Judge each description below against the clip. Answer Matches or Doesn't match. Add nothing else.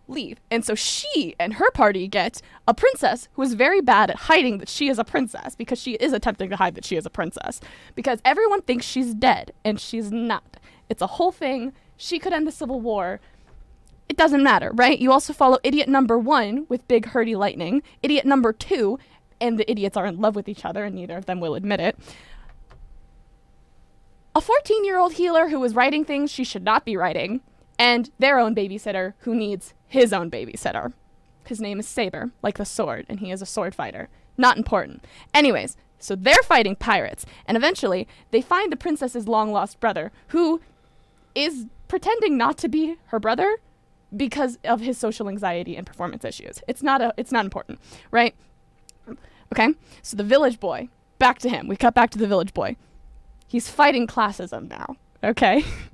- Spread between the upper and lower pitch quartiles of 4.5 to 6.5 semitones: Matches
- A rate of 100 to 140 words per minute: Doesn't match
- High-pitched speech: Matches